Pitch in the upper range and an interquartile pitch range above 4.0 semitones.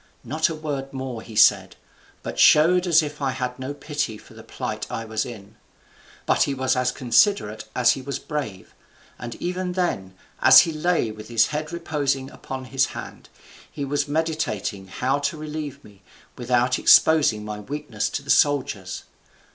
No: low, 135 Hz; average, 4.9 semitones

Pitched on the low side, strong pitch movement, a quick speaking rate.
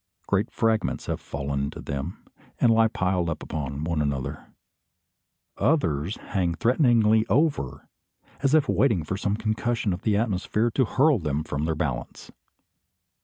No: low, 100 Hz; wide, 6.9 semitones; average, 140 wpm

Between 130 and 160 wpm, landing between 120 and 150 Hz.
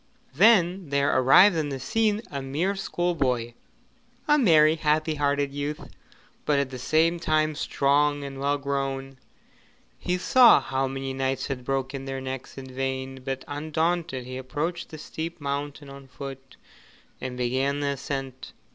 Yes: average, 150 wpm; medium, 140 Hz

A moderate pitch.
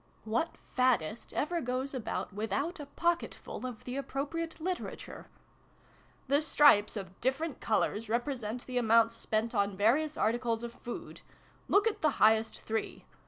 No: high, 245 Hz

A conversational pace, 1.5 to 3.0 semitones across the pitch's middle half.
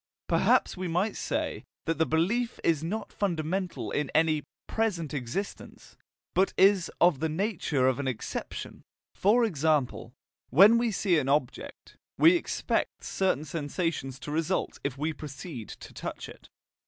No: average, 145 wpm; average, 4.9 semitones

